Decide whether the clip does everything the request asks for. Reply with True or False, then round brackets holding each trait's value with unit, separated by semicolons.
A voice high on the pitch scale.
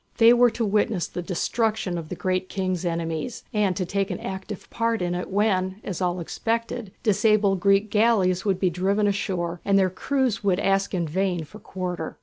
True (195 Hz)